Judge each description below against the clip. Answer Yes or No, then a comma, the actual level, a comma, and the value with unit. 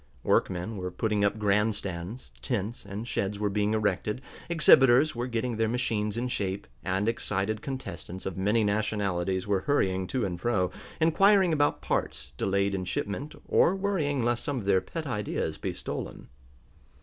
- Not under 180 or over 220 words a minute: No, average, 160 wpm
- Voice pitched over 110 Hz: No, low, 105 Hz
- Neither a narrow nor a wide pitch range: Yes, average, 4.2 semitones